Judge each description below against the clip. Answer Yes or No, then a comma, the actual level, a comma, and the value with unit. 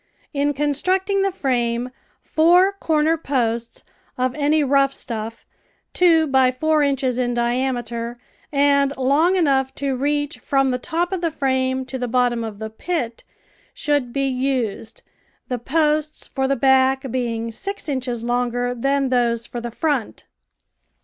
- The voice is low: No, very high, 265 Hz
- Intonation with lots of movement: No, average, 3.4 semitones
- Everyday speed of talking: Yes, average, 145 wpm